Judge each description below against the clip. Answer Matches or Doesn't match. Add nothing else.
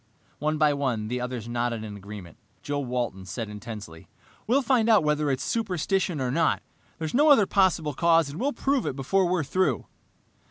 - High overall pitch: Doesn't match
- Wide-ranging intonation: Matches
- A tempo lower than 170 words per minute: Doesn't match